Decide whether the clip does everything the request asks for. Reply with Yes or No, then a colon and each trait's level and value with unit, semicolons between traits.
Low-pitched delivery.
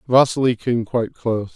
Yes: low, 120 Hz